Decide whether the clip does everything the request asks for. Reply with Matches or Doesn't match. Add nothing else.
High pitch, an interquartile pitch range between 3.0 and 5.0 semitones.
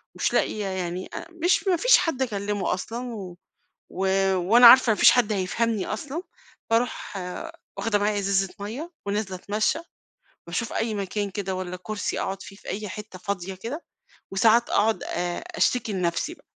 Matches